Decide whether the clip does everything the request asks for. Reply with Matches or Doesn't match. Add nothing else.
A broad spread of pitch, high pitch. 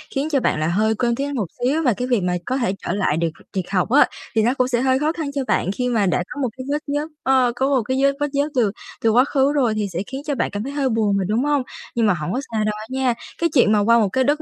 Doesn't match